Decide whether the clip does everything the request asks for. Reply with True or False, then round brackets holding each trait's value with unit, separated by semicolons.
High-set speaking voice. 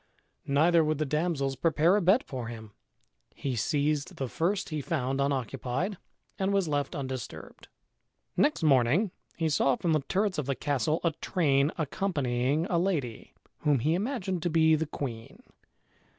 False (150 Hz)